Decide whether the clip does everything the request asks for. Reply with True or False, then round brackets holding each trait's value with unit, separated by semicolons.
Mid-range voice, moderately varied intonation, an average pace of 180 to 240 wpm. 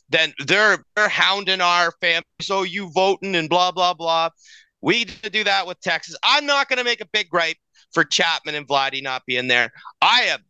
True (180 Hz; 3.6 semitones; 200 wpm)